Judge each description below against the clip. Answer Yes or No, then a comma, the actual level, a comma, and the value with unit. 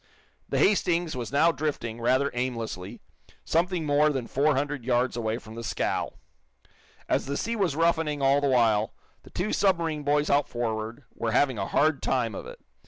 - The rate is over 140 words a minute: Yes, average, 175 wpm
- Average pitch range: Yes, average, 4.6 semitones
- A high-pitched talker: No, medium, 140 Hz